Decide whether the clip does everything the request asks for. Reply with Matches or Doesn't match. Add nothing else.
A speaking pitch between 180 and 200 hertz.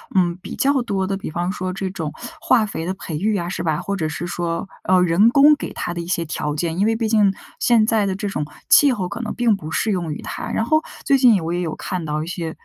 Matches